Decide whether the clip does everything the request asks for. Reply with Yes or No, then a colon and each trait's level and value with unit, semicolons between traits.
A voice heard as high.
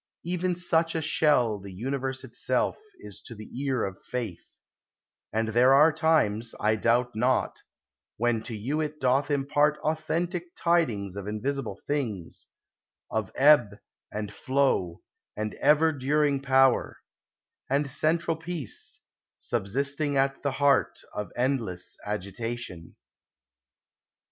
No: low, 135 Hz